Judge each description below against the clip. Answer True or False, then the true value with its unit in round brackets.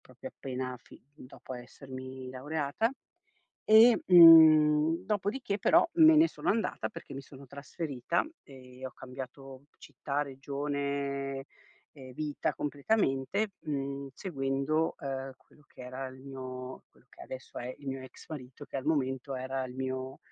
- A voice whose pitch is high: False (140 Hz)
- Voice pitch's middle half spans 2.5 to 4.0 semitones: True (2.8 semitones)